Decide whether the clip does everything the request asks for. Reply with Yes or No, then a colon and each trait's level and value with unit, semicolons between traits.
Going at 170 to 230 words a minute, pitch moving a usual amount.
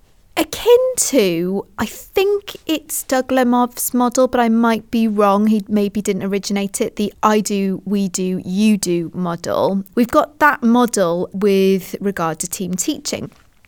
No: average, 155 wpm; average, 4.2 semitones